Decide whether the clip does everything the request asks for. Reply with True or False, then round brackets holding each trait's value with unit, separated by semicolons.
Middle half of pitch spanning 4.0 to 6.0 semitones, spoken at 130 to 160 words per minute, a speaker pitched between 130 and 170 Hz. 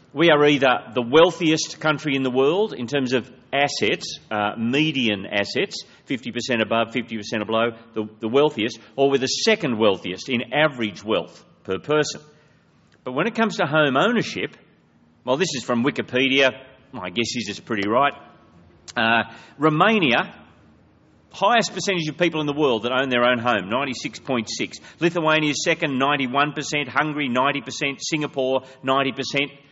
True (4.6 semitones; 150 wpm; 135 Hz)